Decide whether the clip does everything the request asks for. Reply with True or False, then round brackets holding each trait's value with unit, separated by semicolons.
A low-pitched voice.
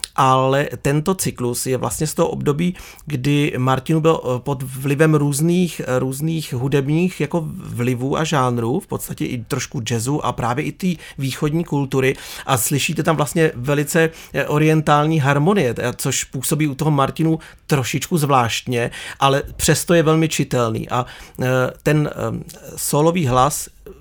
False (145 Hz)